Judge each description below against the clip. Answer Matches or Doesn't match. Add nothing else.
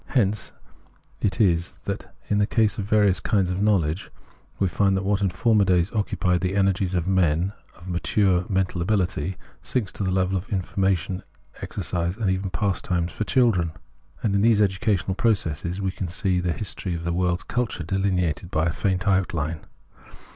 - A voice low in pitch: Matches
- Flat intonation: Matches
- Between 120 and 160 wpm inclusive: Doesn't match